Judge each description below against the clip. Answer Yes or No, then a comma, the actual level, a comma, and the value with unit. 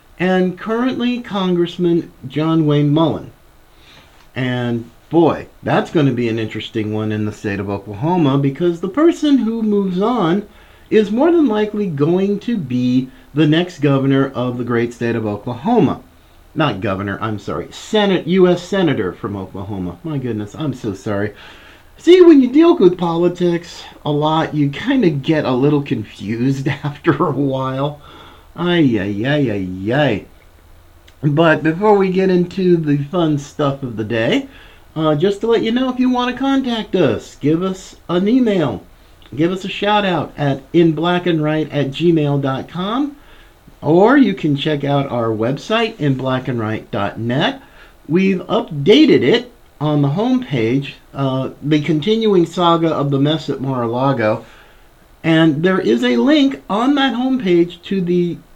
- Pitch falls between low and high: Yes, medium, 155 Hz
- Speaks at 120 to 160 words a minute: Yes, average, 155 wpm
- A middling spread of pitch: No, wide, 6.5 semitones